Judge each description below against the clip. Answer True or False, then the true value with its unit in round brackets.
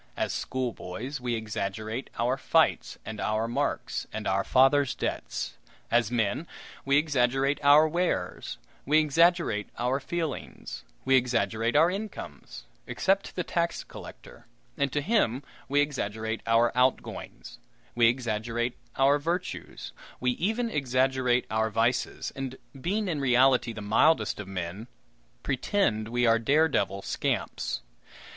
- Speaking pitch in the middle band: False (125 Hz)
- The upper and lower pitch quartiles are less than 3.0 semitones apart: False (4.4 semitones)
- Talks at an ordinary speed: False (130 wpm)